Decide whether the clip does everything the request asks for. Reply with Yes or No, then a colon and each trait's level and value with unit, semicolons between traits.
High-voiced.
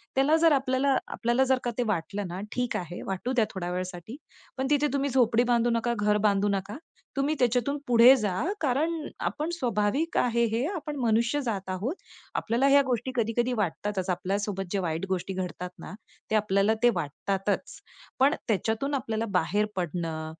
Yes: high, 225 Hz